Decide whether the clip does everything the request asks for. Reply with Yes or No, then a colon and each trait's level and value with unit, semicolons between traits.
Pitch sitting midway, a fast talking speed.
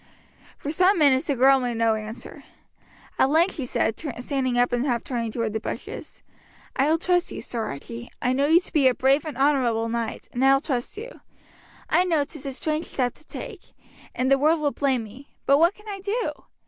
No: very high, 270 Hz; fast, 215 wpm